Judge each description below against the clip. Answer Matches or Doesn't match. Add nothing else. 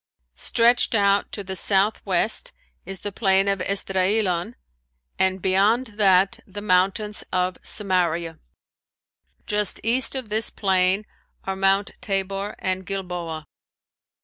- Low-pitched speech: Doesn't match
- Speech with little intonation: Matches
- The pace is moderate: Doesn't match